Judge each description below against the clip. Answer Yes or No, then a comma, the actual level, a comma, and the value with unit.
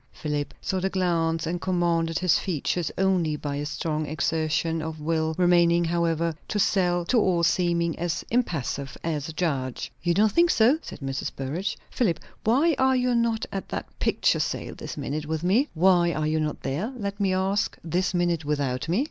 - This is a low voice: No, medium, 170 Hz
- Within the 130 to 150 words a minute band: No, average, 180 wpm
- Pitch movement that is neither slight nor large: Yes, average, 3.3 semitones